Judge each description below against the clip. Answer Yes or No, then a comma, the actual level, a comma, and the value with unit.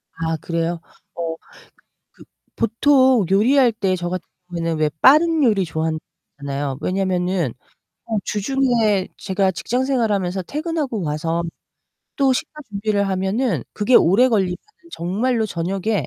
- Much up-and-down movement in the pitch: Yes, wide, 6.0 semitones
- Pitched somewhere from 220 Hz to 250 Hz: No, high, 195 Hz